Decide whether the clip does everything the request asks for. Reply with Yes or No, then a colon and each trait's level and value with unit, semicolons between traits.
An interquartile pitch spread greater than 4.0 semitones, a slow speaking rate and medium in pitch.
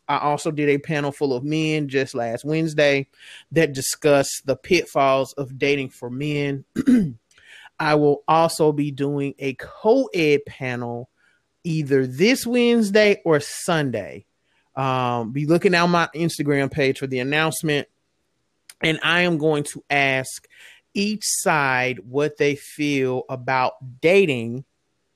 No: average, 3.3 semitones; slow, 130 wpm; medium, 145 Hz